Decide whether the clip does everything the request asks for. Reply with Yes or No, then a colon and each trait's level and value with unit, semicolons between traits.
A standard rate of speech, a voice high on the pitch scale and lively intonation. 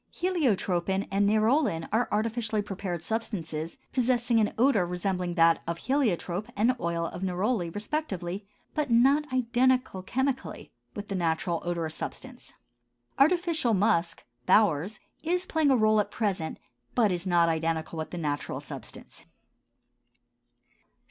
No: slow, 130 wpm; high, 205 Hz; wide, 6.1 semitones